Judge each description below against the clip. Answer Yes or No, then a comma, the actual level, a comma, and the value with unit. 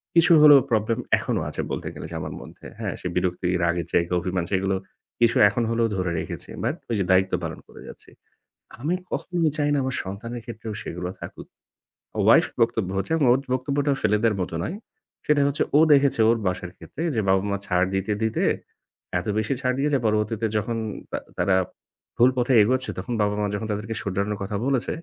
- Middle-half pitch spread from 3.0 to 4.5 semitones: No, average, 5.1 semitones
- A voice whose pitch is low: Yes, low, 110 Hz